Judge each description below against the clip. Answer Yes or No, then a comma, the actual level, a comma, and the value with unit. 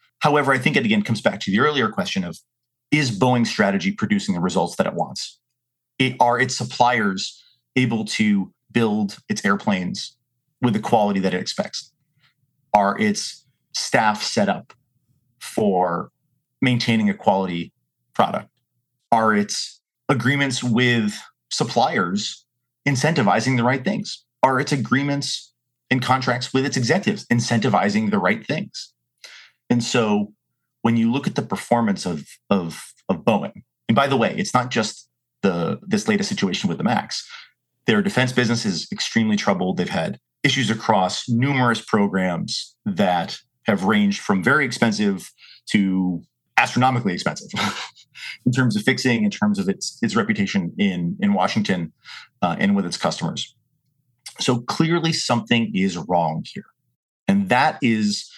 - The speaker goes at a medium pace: Yes, average, 145 wpm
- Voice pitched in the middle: No, low, 125 Hz